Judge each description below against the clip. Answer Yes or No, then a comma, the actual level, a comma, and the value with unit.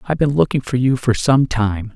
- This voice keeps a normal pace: No, fast, 245 wpm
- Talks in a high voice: No, low, 125 Hz